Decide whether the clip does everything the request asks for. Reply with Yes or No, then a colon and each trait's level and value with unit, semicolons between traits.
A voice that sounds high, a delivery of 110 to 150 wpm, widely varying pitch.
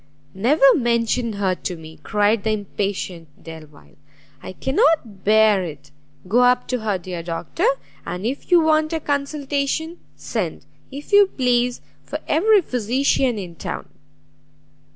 Yes: high, 235 Hz; slow, 135 wpm; wide, 6.7 semitones